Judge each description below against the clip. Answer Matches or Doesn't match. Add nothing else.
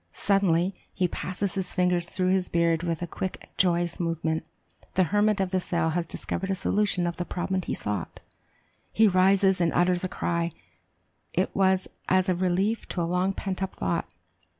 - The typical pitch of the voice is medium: Matches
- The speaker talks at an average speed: Matches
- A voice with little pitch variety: Matches